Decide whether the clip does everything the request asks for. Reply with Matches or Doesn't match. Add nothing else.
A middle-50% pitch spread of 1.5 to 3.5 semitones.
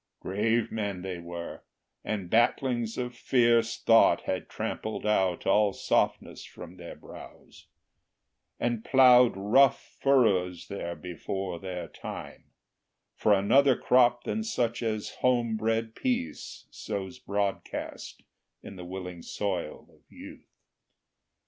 Doesn't match